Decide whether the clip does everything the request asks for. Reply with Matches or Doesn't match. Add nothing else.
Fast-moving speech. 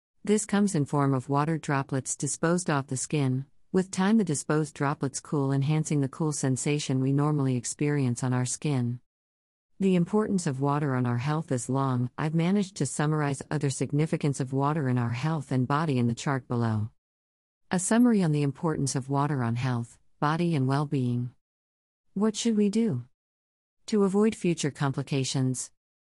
Doesn't match